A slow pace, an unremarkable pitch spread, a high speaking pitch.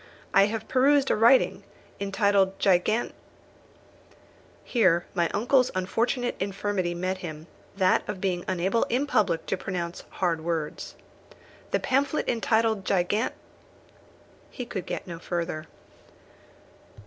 Yes: slow, 125 wpm; average, 4.4 semitones; high, 195 Hz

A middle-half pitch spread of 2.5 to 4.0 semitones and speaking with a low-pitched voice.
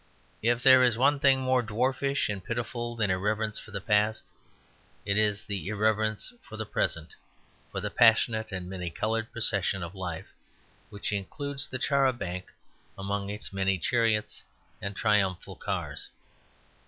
Yes: average, 3.4 semitones; low, 110 Hz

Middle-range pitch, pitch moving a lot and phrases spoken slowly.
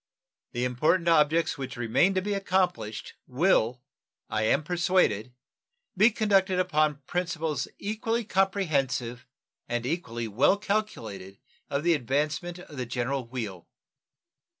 Yes: medium, 150 Hz; wide, 7.1 semitones; slow, 120 wpm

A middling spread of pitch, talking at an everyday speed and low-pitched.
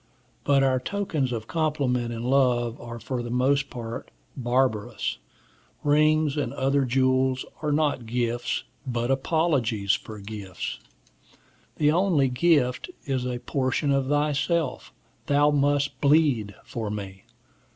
No: average, 3.3 semitones; slow, 125 wpm; low, 130 Hz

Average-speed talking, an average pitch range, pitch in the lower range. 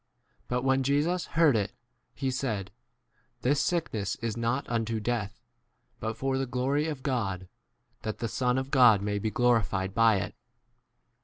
Yes: average, 160 wpm; average, 3.7 semitones; low, 120 Hz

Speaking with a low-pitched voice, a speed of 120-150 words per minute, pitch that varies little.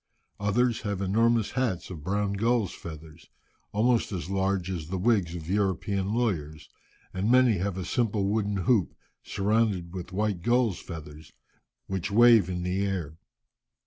No: low, 100 Hz; average, 145 wpm; average, 3.7 semitones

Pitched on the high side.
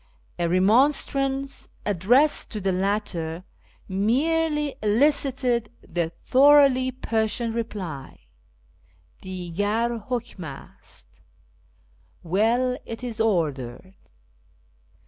Yes: high, 220 Hz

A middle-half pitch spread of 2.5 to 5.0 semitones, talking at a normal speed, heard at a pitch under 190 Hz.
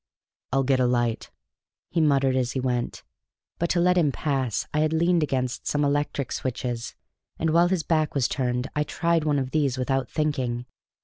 Yes: average, 3.5 semitones; average, 185 wpm; medium, 140 Hz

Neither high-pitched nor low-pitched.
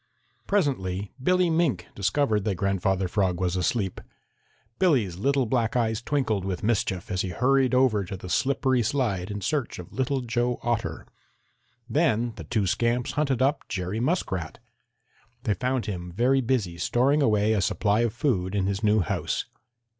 No: low, 110 Hz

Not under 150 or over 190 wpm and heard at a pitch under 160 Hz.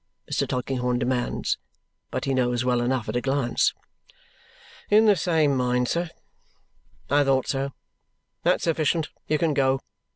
No: average, 140 wpm; low, 135 Hz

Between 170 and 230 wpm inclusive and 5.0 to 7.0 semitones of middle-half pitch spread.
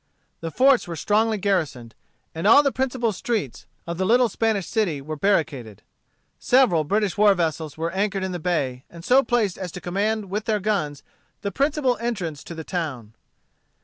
Yes: average, 180 wpm; wide, 5.4 semitones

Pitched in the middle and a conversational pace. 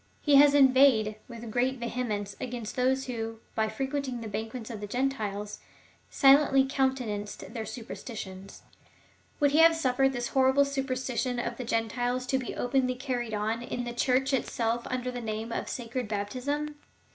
No: high, 245 Hz; average, 160 wpm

